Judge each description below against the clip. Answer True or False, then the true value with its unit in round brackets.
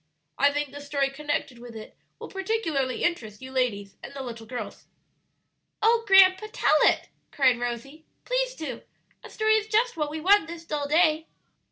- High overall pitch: True (295 Hz)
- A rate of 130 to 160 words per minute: False (175 wpm)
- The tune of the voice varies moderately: False (6.7 semitones)